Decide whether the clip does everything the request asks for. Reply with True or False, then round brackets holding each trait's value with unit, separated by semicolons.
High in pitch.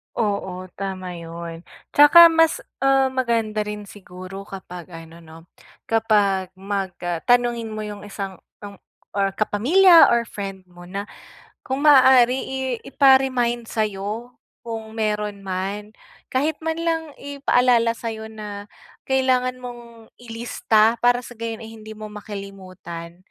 True (215 Hz)